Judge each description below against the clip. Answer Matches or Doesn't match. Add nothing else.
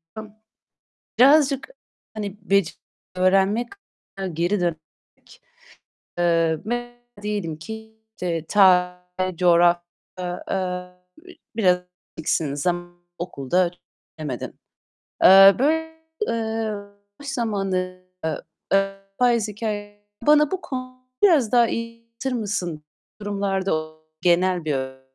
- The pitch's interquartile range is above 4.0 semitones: Matches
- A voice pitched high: Matches